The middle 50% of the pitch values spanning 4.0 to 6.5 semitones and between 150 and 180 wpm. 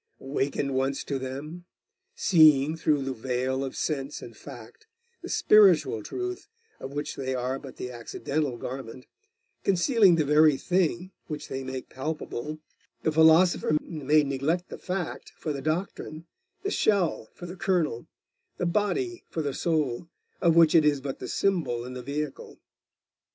Yes: average, 4.4 semitones; average, 155 wpm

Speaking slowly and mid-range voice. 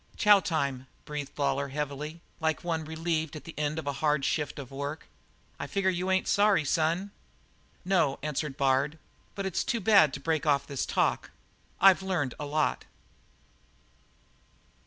No: average, 155 wpm; medium, 155 Hz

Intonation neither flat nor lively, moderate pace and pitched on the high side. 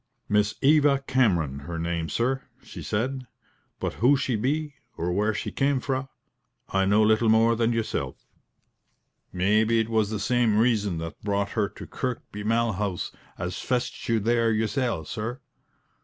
No: average, 3.5 semitones; average, 155 wpm; low, 110 Hz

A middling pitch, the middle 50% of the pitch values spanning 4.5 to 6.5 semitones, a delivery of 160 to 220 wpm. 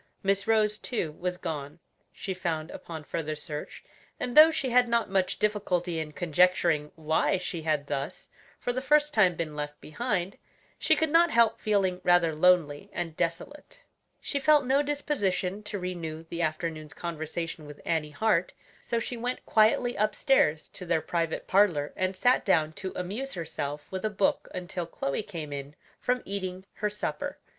Yes: medium, 180 Hz; average, 5.2 semitones; average, 170 wpm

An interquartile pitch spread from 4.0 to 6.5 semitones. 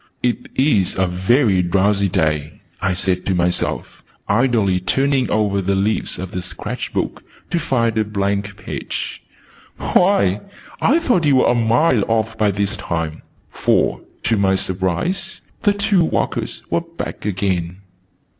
Yes: wide, 5.6 semitones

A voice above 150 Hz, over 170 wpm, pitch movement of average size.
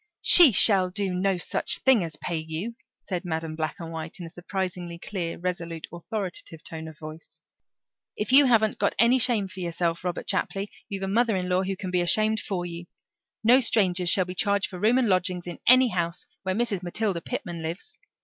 Yes: medium, 185 Hz; fast, 205 wpm; average, 3.7 semitones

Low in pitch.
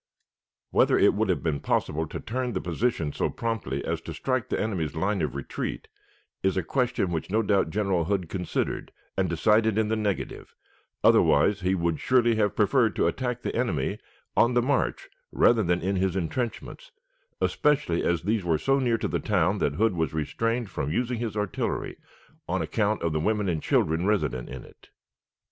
Yes: low, 100 Hz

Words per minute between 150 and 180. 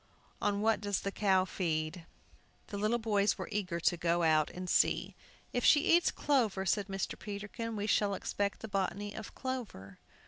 Yes: average, 175 wpm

